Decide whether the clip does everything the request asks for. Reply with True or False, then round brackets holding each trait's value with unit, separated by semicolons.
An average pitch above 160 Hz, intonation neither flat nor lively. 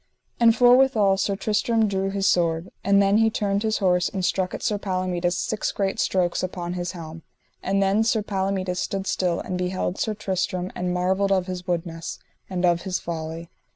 False (190 Hz; 1.9 semitones)